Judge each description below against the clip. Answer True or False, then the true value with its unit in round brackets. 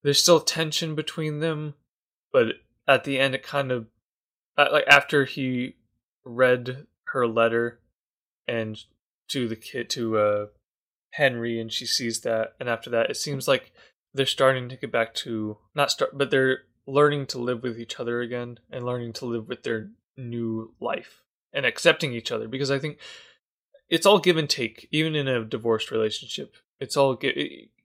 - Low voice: True (125 Hz)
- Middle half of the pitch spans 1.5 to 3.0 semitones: False (3.6 semitones)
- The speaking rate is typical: True (175 wpm)